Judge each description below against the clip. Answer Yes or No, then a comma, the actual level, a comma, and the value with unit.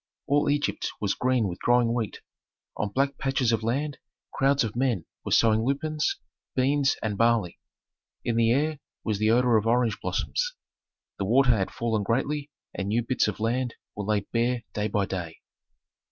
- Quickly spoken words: No, average, 170 wpm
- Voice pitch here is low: Yes, low, 120 Hz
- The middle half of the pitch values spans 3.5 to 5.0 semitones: Yes, average, 3.9 semitones